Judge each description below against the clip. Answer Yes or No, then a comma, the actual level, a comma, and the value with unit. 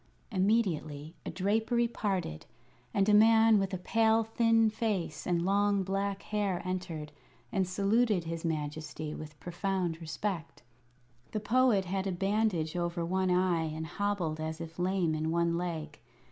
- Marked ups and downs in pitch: No, average, 3.9 semitones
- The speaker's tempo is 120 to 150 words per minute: Yes, average, 145 wpm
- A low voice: No, medium, 185 Hz